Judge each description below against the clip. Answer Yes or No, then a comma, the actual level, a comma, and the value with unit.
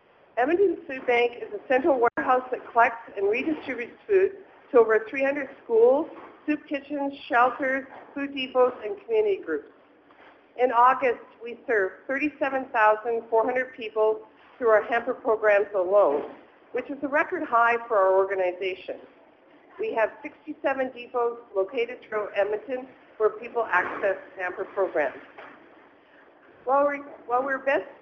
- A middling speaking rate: No, slow, 125 wpm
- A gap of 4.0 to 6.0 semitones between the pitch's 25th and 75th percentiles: Yes, average, 5.0 semitones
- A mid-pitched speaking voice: No, very high, 255 Hz